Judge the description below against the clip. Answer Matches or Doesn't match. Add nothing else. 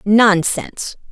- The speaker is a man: Doesn't match